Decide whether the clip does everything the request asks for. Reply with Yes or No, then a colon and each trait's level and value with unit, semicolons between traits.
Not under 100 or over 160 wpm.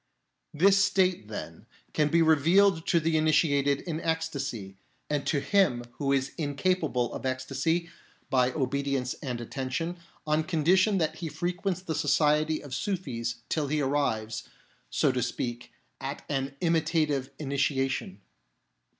Yes: slow, 135 wpm